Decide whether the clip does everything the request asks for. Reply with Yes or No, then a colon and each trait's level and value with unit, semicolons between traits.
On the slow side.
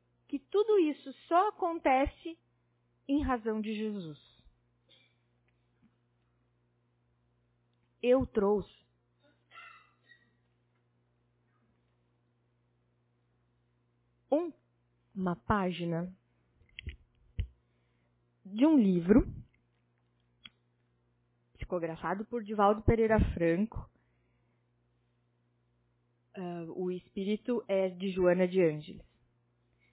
Yes: slow, 60 wpm